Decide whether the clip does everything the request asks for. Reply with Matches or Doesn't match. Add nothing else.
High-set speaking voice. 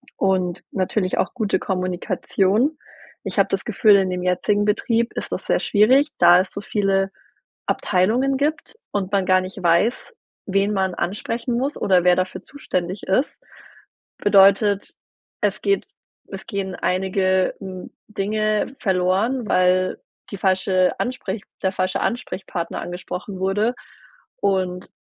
Matches